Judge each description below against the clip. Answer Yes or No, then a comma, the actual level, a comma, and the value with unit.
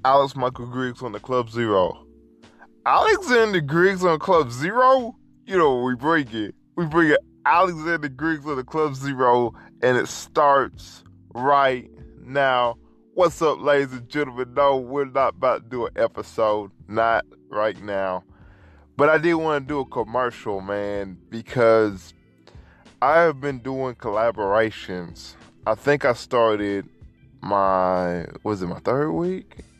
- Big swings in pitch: Yes, wide, 6.1 semitones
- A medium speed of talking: Yes, average, 145 wpm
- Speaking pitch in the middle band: No, low, 125 Hz